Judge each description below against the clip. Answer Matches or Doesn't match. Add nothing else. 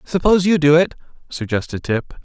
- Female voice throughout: Doesn't match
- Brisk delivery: Doesn't match